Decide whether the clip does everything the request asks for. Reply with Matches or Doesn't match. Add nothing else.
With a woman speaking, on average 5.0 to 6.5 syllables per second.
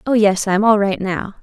Matches